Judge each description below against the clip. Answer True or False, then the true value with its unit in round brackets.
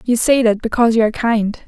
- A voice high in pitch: True (230 Hz)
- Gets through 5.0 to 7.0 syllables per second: True (6.5 syllables/s)